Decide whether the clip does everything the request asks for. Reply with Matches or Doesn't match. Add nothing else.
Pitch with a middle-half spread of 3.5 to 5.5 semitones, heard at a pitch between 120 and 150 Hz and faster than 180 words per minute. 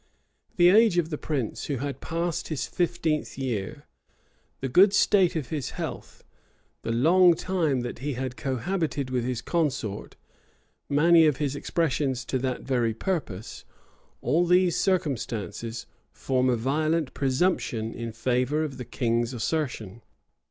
Doesn't match